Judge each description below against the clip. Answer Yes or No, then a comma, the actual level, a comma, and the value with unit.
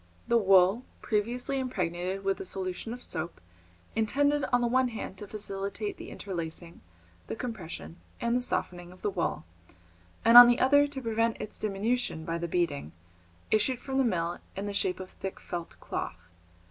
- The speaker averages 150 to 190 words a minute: Yes, average, 170 wpm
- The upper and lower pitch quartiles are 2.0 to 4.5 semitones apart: No, average, 5.3 semitones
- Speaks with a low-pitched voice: No, high, 205 Hz